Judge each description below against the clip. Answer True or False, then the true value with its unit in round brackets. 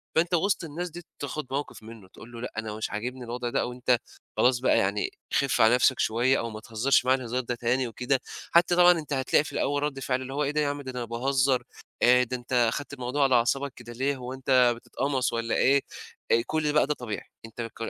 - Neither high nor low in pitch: False (130 Hz)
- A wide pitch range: False (2.9 semitones)